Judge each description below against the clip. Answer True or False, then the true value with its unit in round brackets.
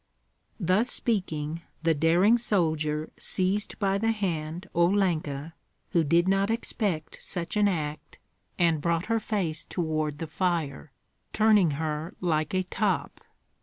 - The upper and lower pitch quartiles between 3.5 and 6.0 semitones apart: True (4.1 semitones)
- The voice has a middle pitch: True (170 Hz)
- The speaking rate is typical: False (130 wpm)